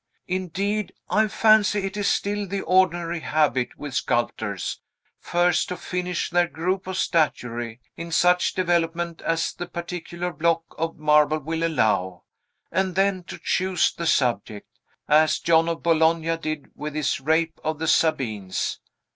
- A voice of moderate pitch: Yes, medium, 165 Hz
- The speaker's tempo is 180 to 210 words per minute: No, average, 145 wpm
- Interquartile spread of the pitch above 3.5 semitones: No, average, 2.9 semitones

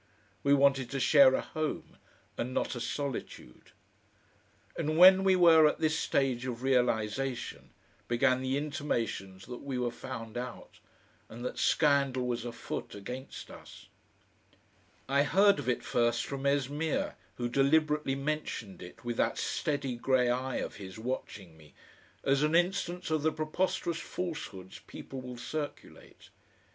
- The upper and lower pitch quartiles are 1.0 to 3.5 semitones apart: No, average, 3.9 semitones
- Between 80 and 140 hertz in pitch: Yes, low, 135 Hz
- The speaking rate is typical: Yes, average, 145 wpm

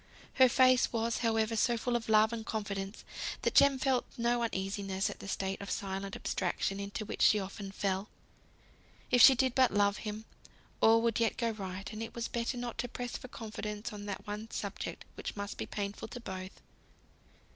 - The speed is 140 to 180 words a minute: No, average, 190 wpm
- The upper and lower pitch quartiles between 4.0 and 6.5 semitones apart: No, average, 2.9 semitones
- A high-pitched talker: Yes, high, 220 Hz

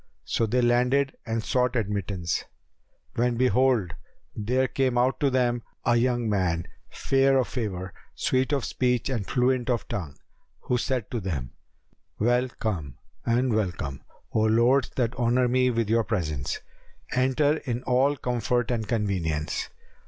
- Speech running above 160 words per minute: No, average, 145 wpm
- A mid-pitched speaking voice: No, low, 120 Hz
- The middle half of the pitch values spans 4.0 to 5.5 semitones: No, average, 3.5 semitones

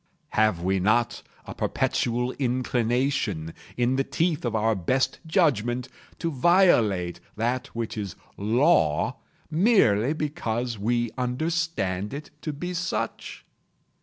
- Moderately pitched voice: No, low, 120 Hz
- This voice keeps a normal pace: No, slow, 115 wpm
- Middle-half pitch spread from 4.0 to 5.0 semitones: No, wide, 5.5 semitones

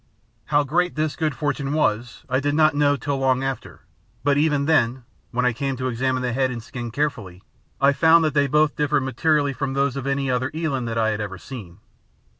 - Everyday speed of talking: No, fast, 215 wpm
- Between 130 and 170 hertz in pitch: Yes, low, 135 Hz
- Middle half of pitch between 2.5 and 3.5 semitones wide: Yes, average, 2.8 semitones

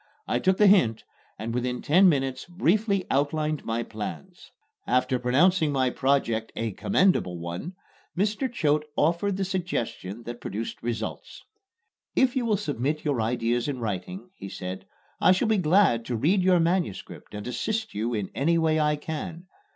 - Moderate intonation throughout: No, wide, 7.8 semitones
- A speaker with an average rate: Yes, average, 160 wpm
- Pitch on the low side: No, medium, 150 Hz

